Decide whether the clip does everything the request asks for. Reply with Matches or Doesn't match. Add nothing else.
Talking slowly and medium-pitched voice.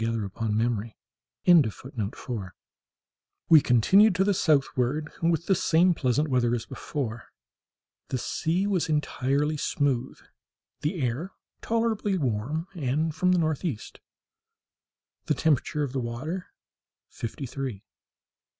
Matches